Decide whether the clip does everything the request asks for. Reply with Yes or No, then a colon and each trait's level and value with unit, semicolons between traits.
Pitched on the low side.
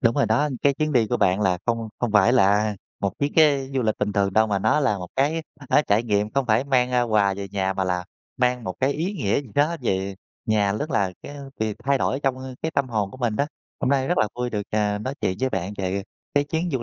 Yes: low, 115 Hz